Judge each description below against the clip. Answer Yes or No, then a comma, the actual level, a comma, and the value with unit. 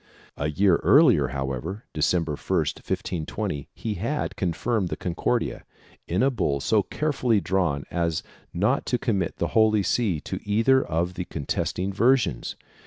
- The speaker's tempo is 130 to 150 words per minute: Yes, average, 145 wpm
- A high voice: No, very low, 95 Hz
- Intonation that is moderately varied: No, wide, 6.0 semitones